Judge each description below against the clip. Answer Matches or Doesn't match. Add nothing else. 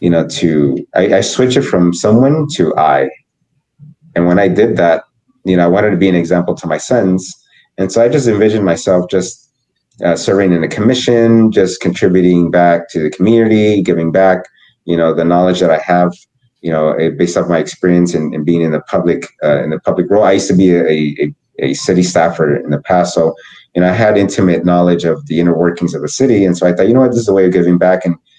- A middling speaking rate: Doesn't match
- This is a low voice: Matches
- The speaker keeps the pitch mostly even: Doesn't match